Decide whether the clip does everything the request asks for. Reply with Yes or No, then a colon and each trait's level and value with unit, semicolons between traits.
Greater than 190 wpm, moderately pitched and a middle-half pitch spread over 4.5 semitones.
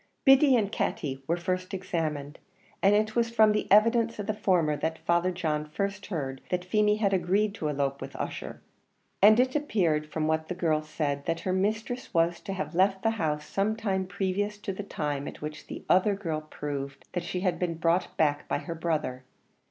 Yes: average, 200 wpm; medium, 180 Hz; average, 5.0 semitones